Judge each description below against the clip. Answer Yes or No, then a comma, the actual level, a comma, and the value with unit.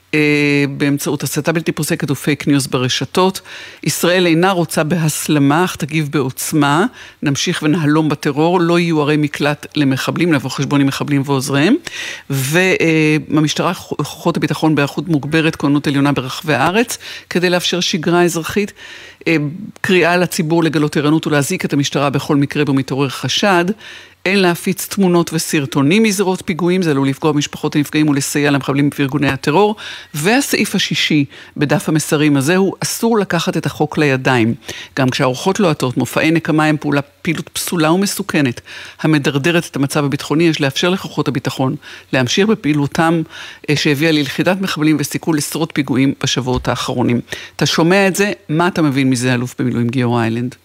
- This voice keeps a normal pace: Yes, average, 140 wpm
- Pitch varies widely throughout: No, average, 3.3 semitones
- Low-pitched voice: No, medium, 155 Hz